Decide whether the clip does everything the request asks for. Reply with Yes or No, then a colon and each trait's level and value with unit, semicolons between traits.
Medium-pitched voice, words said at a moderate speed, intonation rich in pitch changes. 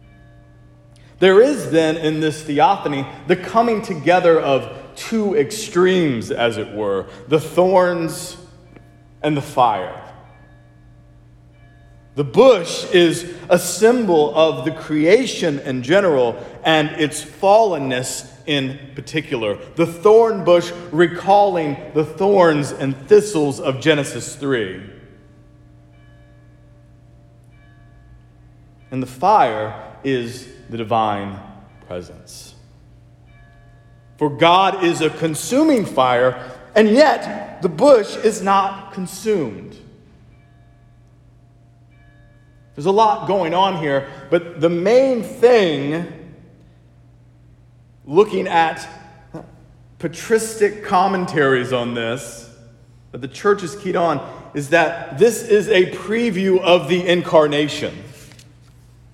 No: medium, 150 Hz; slow, 100 wpm; wide, 7.0 semitones